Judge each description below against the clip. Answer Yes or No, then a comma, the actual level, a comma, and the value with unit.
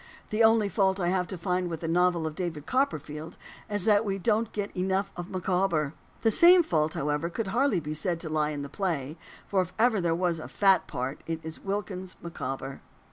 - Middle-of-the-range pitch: Yes, medium, 180 Hz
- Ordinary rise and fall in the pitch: Yes, average, 4.1 semitones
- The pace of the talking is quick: Yes, fast, 210 wpm